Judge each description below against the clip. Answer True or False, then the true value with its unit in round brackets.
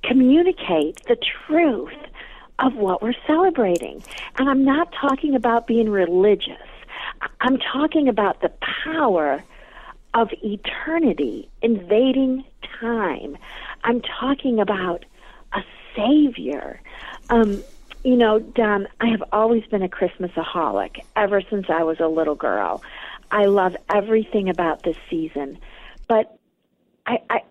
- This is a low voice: False (230 Hz)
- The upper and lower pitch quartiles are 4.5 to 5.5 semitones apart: True (4.9 semitones)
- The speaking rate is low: True (120 wpm)